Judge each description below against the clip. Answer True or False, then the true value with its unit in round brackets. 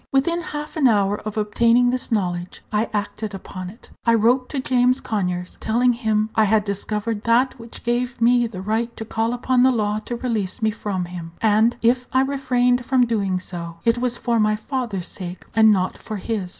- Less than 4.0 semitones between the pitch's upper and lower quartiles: True (3.1 semitones)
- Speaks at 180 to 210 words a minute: True (200 wpm)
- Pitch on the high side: True (225 Hz)